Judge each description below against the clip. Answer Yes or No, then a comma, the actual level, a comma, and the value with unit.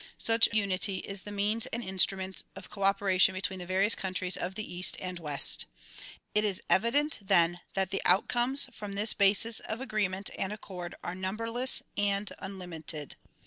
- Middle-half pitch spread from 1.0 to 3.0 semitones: Yes, narrow, 2.4 semitones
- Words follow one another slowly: No, average, 165 wpm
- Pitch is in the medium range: No, high, 195 Hz